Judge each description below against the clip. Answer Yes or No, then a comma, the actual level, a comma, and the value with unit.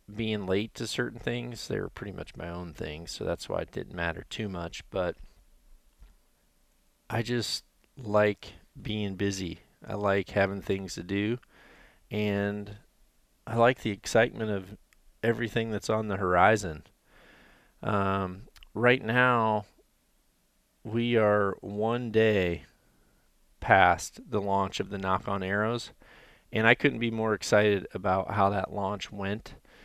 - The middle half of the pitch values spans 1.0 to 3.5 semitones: Yes, average, 2.7 semitones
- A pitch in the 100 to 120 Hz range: Yes, low, 105 Hz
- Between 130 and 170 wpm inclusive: Yes, average, 140 wpm